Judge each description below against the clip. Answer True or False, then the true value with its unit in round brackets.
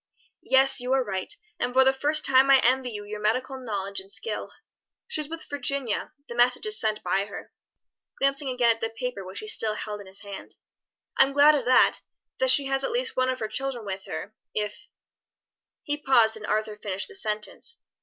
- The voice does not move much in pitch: False (4.3 semitones)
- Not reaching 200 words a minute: False (205 wpm)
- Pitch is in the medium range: False (250 Hz)